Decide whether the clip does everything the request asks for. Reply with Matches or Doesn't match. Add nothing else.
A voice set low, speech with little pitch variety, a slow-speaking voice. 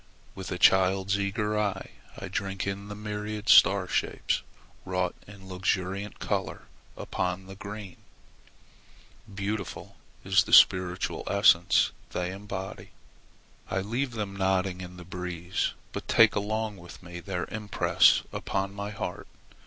Matches